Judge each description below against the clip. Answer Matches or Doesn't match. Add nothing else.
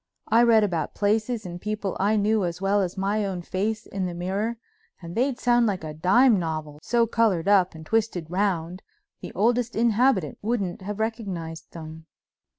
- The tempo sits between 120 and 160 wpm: Doesn't match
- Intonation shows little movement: Doesn't match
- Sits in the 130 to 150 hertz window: Doesn't match